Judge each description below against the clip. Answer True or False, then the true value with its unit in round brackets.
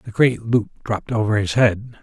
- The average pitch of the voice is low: True (110 Hz)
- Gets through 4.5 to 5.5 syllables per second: True (4.9 syllables/s)